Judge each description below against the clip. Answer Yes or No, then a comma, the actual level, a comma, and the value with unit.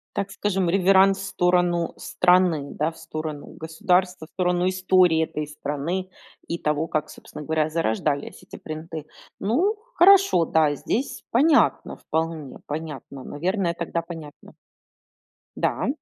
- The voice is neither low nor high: Yes, medium, 170 Hz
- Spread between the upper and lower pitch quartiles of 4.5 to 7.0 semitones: No, average, 3.2 semitones